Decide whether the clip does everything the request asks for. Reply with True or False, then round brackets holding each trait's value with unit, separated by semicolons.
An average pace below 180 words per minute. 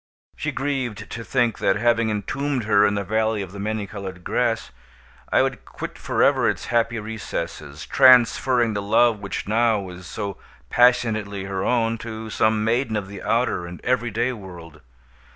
True (165 wpm)